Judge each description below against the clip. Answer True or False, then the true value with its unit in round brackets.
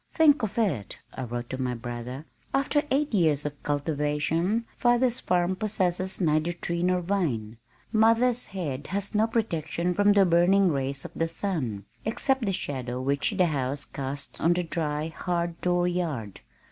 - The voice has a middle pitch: True (170 Hz)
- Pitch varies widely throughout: True (6.0 semitones)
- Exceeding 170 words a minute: False (160 wpm)